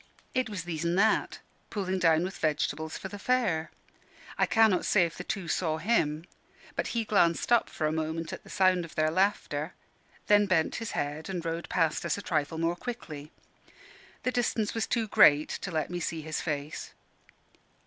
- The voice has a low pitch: No, medium, 170 Hz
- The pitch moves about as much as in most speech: Yes, average, 4.4 semitones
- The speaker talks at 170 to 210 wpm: Yes, average, 190 wpm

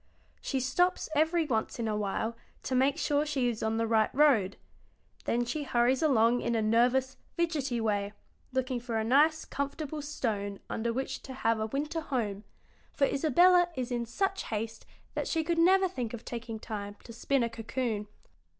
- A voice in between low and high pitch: No, high, 245 Hz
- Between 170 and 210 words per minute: Yes, average, 180 wpm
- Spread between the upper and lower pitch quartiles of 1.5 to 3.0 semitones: No, average, 4.7 semitones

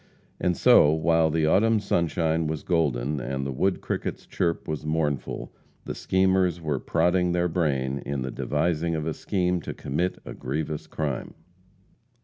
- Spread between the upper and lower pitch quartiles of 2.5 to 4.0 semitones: Yes, average, 3.1 semitones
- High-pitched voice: No, very low, 80 Hz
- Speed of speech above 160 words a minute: No, average, 155 wpm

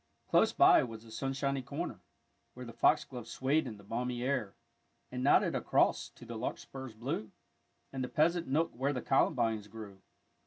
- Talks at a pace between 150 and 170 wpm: Yes, average, 165 wpm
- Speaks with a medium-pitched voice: No, low, 125 Hz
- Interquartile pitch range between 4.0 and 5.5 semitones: No, average, 3.5 semitones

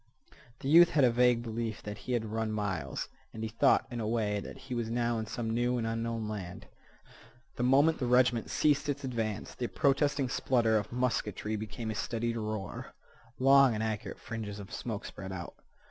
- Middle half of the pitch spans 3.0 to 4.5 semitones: No, narrow, 2.5 semitones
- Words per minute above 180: Yes, average, 190 wpm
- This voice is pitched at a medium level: No, low, 115 Hz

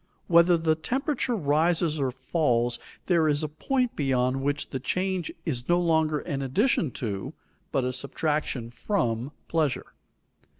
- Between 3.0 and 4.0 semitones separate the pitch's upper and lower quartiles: No, average, 4.8 semitones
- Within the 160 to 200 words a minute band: No, average, 140 wpm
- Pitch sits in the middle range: Yes, medium, 155 Hz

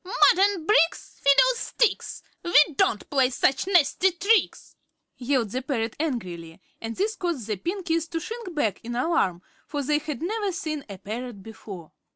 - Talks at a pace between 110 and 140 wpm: No, average, 160 wpm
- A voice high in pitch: Yes, very high, 300 Hz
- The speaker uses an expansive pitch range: Yes, wide, 7.9 semitones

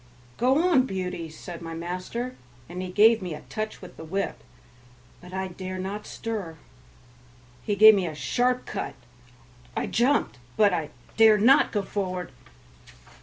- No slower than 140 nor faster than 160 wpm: Yes, average, 155 wpm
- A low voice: No, high, 195 Hz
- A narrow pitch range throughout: No, average, 3.8 semitones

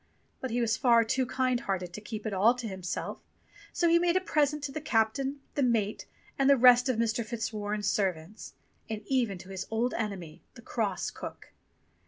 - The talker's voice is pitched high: Yes, high, 230 Hz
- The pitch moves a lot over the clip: No, average, 3.9 semitones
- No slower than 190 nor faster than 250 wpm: Yes, average, 195 wpm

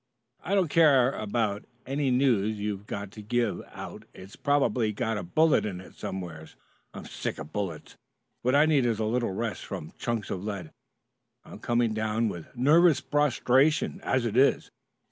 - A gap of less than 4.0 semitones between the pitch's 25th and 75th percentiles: No, average, 5.0 semitones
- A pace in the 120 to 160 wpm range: No, average, 170 wpm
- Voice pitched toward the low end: Yes, low, 115 Hz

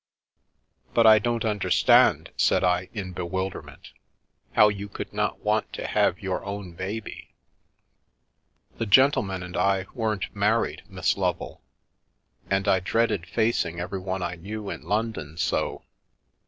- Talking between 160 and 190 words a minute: No, average, 145 wpm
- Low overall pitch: Yes, low, 100 Hz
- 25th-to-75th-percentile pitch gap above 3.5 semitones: No, average, 2.9 semitones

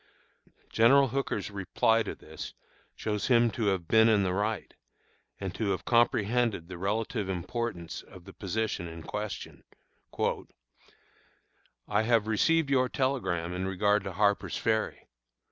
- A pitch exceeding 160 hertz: No, low, 105 Hz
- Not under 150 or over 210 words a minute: No, slow, 135 wpm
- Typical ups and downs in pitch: Yes, average, 3.6 semitones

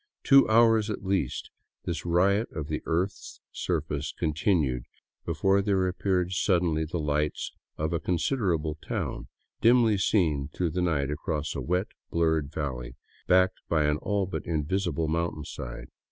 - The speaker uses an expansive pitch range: No, average, 4.0 semitones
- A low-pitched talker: Yes, very low, 85 Hz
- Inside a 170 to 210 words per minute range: No, average, 145 wpm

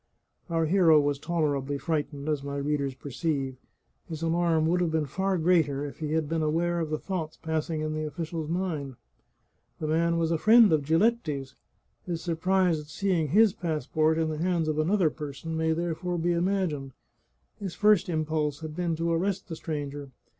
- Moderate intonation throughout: No, narrow, 2.3 semitones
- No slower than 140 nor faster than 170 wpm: No, average, 180 wpm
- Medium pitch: Yes, medium, 160 Hz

